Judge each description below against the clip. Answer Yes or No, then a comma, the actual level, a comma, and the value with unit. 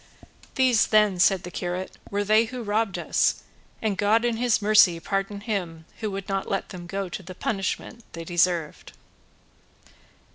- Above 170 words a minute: No, average, 160 wpm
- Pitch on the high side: Yes, high, 195 Hz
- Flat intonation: No, average, 3.2 semitones